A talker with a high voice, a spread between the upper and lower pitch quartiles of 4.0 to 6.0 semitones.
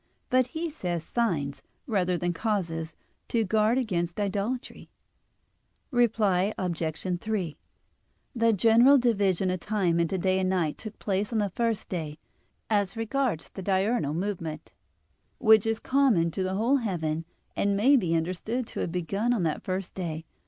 Yes: high, 195 Hz; average, 4.6 semitones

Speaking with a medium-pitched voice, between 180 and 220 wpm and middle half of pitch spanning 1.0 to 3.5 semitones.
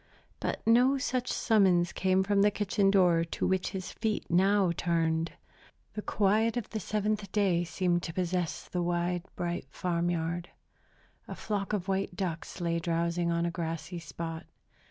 No: medium, 180 Hz; average, 160 wpm; average, 3.0 semitones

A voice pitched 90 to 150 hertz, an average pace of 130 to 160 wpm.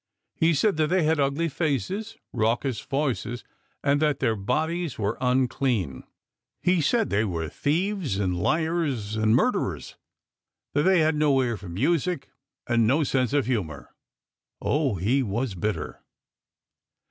Yes: low, 135 Hz; average, 140 wpm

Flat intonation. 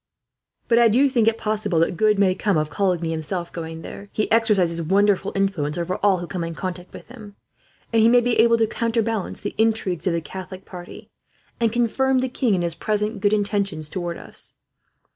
No: average, 4.3 semitones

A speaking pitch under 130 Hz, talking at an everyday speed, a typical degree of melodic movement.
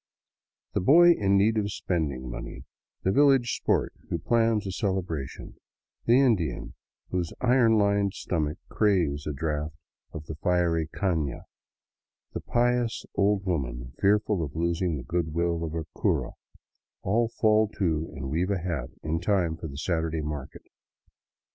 Yes: very low, 85 Hz; average, 145 wpm; average, 5.0 semitones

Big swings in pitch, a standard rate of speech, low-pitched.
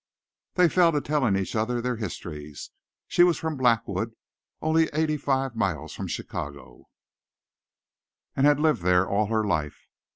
Yes: wide, 8.0 semitones; average, 150 wpm; low, 120 Hz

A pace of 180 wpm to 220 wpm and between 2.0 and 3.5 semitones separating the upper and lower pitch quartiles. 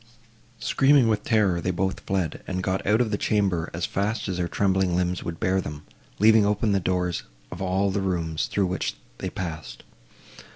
Yes: average, 190 wpm; narrow, 2.6 semitones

